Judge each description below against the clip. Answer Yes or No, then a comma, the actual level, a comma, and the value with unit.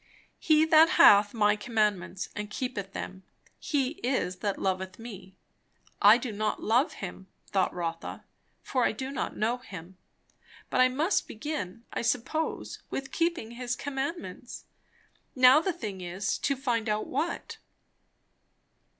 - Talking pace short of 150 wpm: Yes, average, 140 wpm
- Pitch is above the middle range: Yes, high, 230 Hz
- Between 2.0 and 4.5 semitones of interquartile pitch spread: No, wide, 5.4 semitones